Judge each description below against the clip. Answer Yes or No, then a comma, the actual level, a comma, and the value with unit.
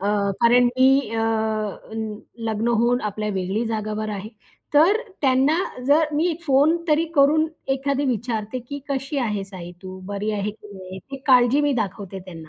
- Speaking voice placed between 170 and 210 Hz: No, high, 235 Hz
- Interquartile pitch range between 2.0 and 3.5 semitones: No, average, 5.2 semitones